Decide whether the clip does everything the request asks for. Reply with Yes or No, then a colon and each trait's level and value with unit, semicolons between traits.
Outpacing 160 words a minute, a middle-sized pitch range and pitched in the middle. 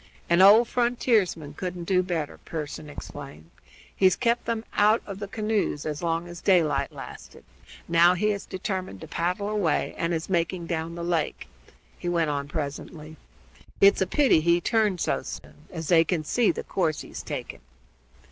Yes: average, 170 wpm; average, 4.0 semitones; medium, 175 Hz